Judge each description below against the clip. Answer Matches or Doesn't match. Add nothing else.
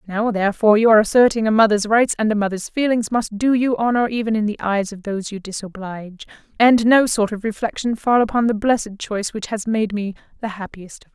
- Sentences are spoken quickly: Matches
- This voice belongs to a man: Doesn't match